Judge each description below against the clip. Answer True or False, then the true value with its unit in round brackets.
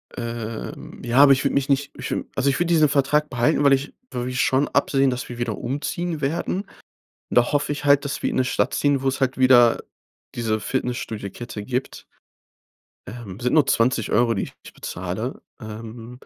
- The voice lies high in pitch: False (130 Hz)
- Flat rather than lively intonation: False (3.1 semitones)